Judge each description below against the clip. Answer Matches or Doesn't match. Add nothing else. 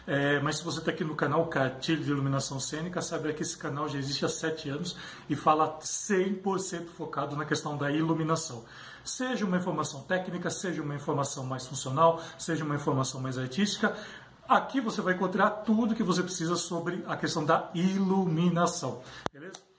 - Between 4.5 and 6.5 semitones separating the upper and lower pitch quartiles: Doesn't match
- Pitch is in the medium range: Matches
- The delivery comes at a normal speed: Matches